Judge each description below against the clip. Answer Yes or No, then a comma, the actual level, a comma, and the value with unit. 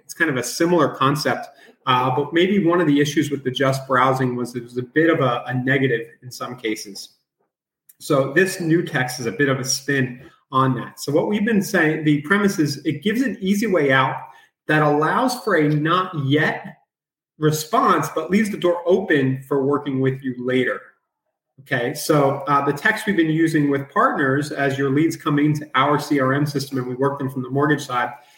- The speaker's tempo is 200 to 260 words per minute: Yes, fast, 205 wpm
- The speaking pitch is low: No, medium, 145 Hz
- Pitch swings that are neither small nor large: Yes, average, 3.6 semitones